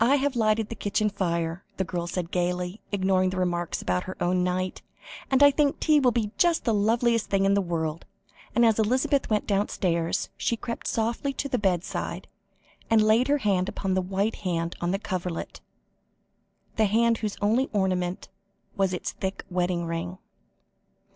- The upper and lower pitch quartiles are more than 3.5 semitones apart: Yes, average, 4.1 semitones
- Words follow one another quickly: No, average, 175 wpm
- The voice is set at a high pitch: Yes, high, 195 Hz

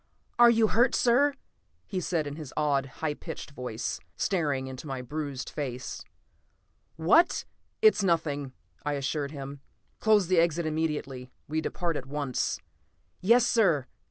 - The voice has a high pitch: No, medium, 150 Hz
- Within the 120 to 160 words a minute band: Yes, average, 140 wpm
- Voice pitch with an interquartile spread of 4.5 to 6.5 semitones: Yes, average, 4.9 semitones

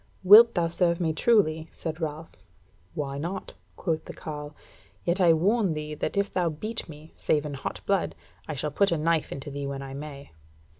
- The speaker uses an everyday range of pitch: Yes, average, 3.3 semitones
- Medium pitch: Yes, medium, 160 Hz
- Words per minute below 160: No, average, 195 wpm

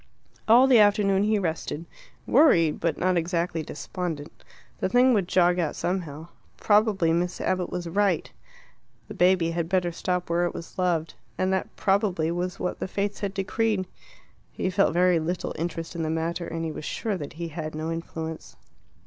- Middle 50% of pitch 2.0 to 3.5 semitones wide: Yes, average, 2.8 semitones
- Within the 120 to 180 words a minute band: Yes, average, 175 wpm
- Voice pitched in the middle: Yes, medium, 175 Hz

